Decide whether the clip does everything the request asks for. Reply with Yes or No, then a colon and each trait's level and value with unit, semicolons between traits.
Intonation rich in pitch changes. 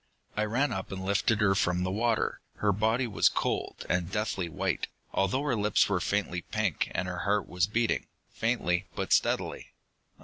No: average, 3.3 semitones